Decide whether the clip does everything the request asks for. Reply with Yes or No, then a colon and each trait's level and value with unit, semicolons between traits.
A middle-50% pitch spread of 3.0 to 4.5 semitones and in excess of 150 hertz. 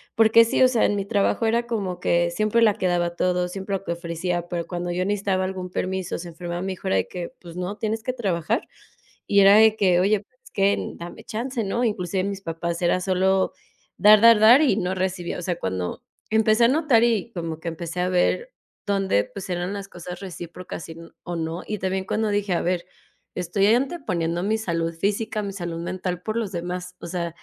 Yes: average, 3.4 semitones; high, 190 Hz